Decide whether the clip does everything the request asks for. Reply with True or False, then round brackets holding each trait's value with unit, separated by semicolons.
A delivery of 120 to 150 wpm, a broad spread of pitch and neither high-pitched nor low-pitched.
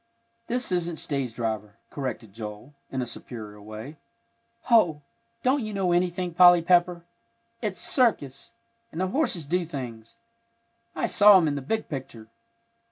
True (145 wpm; 7.3 semitones; 160 Hz)